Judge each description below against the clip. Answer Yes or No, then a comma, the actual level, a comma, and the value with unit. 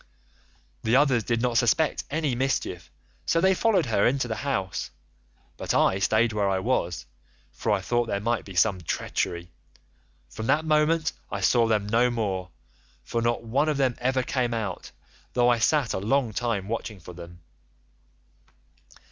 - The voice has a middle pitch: No, low, 115 Hz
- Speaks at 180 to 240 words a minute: No, average, 165 wpm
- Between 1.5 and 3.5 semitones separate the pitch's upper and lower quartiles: No, average, 4.8 semitones